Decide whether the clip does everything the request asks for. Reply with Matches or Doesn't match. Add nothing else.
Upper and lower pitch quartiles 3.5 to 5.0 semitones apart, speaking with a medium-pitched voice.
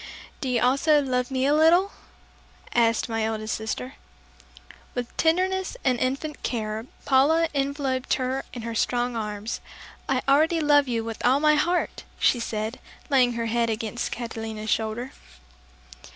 Doesn't match